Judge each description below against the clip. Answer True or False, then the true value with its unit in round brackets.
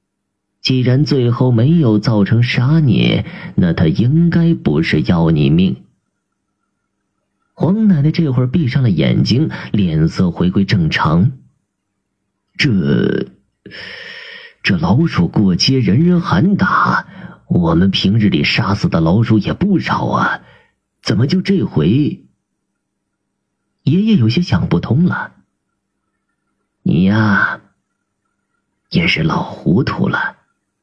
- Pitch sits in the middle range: True (160 Hz)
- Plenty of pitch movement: True (6.6 semitones)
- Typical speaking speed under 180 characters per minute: True (160 characters per minute)